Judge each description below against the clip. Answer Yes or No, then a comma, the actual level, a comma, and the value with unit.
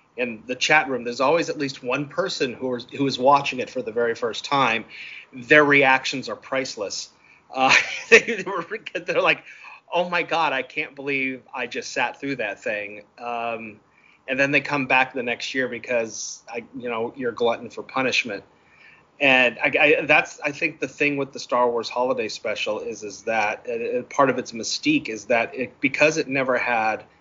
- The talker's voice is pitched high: No, medium, 140 Hz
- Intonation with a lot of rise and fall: Yes, wide, 5.8 semitones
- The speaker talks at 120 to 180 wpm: No, average, 195 wpm